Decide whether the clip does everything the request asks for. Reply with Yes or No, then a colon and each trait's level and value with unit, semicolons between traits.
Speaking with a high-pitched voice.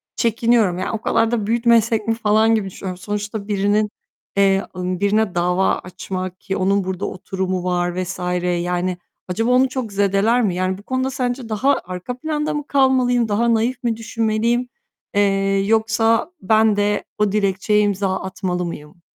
Yes: high, 210 Hz